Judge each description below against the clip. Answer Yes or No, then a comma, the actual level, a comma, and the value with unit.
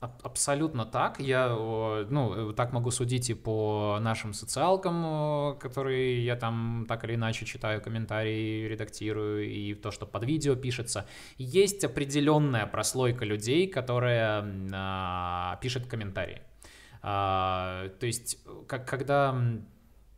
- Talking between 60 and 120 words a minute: Yes, average, 115 wpm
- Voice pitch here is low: Yes, low, 115 Hz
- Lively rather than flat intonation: No, average, 3.5 semitones